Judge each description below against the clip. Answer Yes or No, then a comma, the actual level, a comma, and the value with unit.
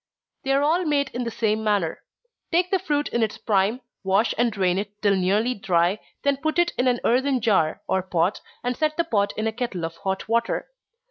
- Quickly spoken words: Yes, fast, 220 wpm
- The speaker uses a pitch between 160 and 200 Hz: No, high, 225 Hz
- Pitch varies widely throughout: Yes, wide, 5.8 semitones